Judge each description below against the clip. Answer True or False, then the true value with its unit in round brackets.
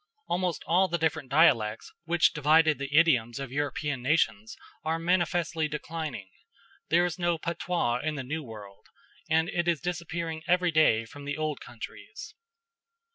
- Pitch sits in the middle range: True (155 Hz)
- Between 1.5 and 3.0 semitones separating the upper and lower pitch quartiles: False (3.8 semitones)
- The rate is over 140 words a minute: True (150 wpm)